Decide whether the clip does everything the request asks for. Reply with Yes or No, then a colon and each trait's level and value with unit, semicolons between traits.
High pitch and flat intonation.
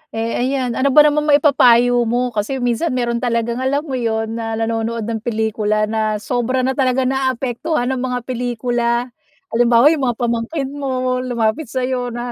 Yes: high, 245 Hz; narrow, 2.1 semitones